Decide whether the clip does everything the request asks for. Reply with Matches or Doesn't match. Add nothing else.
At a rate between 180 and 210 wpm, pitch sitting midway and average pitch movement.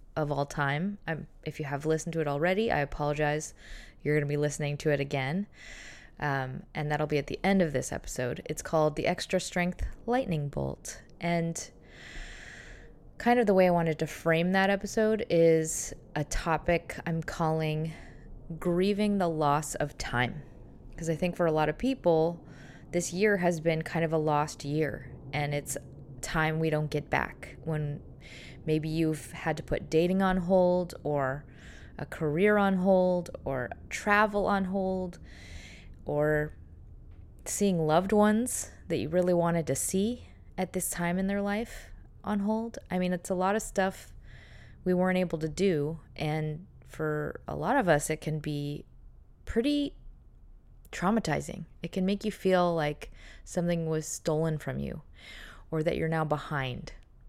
Doesn't match